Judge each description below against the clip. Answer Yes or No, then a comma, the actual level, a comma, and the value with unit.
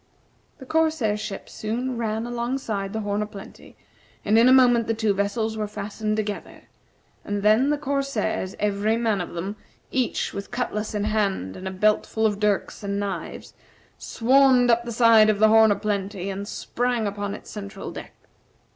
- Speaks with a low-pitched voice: No, high, 215 Hz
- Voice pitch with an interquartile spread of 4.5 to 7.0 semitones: No, narrow, 2.6 semitones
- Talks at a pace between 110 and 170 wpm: No, average, 180 wpm